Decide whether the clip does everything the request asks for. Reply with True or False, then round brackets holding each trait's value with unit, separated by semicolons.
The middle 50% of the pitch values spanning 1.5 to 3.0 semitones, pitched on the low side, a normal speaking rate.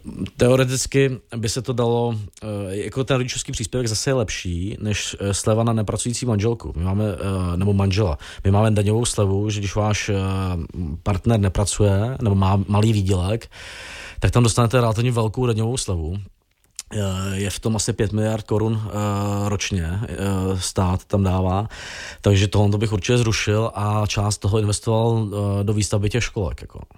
True (2.6 semitones; 105 Hz; 150 wpm)